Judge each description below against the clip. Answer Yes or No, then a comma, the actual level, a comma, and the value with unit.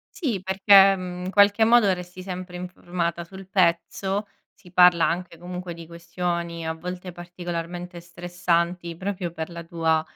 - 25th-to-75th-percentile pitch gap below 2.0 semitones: Yes, narrow, 1.5 semitones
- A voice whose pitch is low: No, medium, 180 Hz